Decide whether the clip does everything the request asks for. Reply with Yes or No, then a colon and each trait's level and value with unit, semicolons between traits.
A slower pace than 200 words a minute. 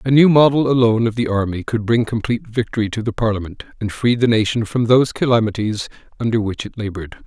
No: fast, 205 wpm